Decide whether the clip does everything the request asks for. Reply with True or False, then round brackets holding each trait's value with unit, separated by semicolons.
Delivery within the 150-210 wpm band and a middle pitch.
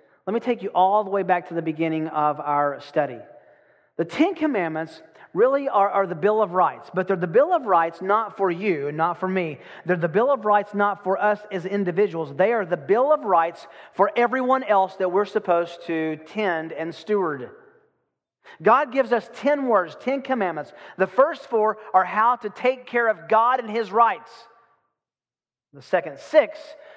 False (190 wpm; 205 Hz)